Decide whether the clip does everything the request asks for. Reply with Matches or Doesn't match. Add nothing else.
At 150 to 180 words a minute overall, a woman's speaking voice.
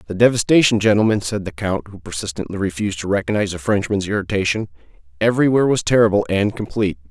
Doesn't match